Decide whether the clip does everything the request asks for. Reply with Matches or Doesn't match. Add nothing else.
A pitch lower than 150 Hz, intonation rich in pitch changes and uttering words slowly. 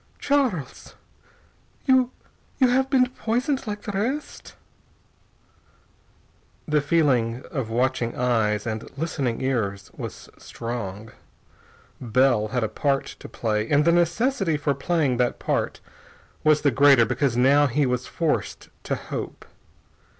Matches